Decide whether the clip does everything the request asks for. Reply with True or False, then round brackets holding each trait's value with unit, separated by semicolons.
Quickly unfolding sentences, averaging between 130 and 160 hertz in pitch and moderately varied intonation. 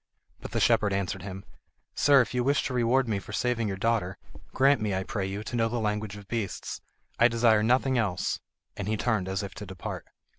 False (220 wpm; 110 Hz; 3.5 semitones)